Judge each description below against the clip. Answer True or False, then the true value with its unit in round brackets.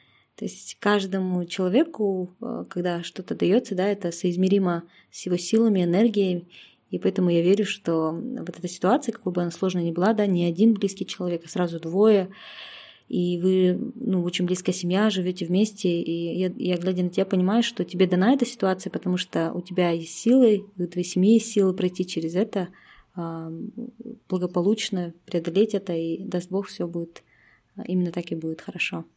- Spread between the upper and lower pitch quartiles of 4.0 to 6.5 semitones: False (2.7 semitones)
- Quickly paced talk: True (170 wpm)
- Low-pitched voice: False (185 Hz)